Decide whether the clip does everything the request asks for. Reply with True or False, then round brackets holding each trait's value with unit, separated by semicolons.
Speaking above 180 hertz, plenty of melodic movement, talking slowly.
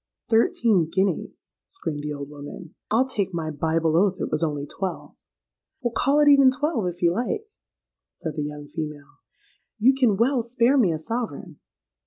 False (190 Hz; 7.4 semitones; 165 wpm)